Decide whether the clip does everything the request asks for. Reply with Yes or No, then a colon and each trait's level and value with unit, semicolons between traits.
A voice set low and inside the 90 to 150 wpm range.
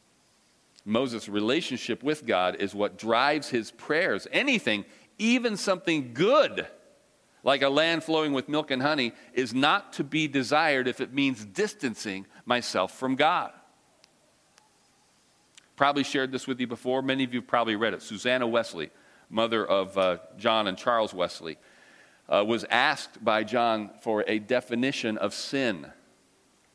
Yes: low, 130 Hz; average, 145 wpm